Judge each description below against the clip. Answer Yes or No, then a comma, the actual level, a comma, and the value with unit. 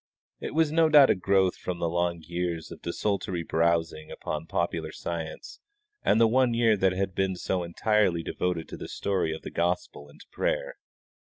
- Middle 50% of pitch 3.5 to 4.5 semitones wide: Yes, average, 4.1 semitones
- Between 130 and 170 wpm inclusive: No, average, 185 wpm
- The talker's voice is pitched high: No, very low, 90 Hz